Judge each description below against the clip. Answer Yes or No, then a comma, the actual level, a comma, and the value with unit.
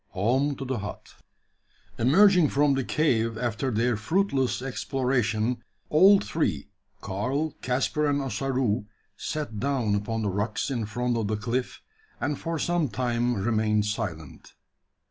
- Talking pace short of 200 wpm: Yes, slow, 135 wpm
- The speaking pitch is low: Yes, low, 125 Hz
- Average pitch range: Yes, average, 4.4 semitones